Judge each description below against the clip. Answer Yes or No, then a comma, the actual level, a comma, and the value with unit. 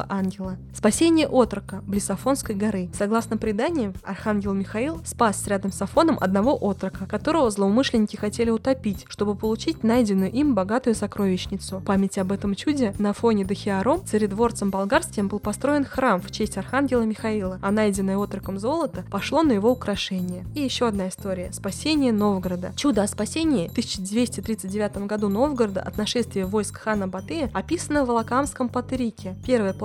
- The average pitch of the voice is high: Yes, high, 215 Hz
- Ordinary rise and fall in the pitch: Yes, average, 4.1 semitones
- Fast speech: No, average, 145 wpm